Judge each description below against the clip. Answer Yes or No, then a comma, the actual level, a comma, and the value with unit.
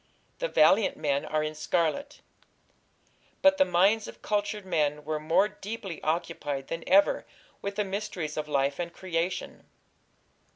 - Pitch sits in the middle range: Yes, medium, 170 Hz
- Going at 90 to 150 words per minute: Yes, average, 140 wpm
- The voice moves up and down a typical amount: Yes, average, 4.9 semitones